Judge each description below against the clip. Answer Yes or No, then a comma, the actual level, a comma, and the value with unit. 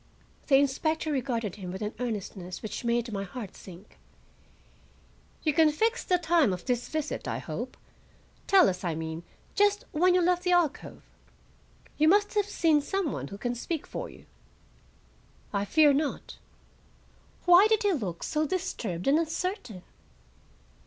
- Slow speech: No, average, 155 wpm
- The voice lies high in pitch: Yes, very high, 290 Hz